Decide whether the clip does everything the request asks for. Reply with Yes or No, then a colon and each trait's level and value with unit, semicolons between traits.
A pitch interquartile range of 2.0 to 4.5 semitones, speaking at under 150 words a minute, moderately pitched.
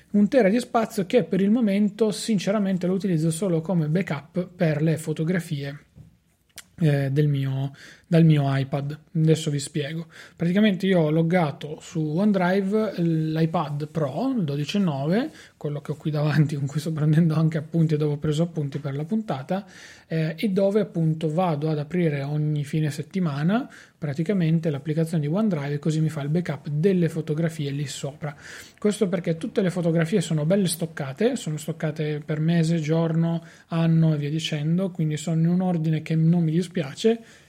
No: average, 3.5 semitones; average, 165 wpm; medium, 165 Hz